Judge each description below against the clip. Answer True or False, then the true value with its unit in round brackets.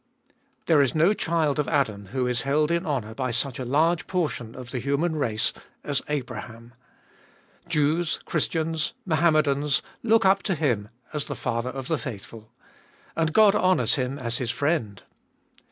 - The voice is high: False (145 Hz)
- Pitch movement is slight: False (4.7 semitones)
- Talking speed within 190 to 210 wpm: False (160 wpm)